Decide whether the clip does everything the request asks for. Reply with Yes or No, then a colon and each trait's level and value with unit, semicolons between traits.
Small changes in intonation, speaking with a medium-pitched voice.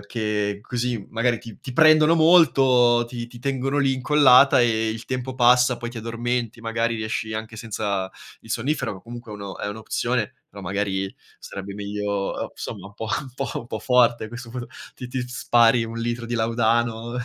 No: narrow, 2.2 semitones; low, 120 Hz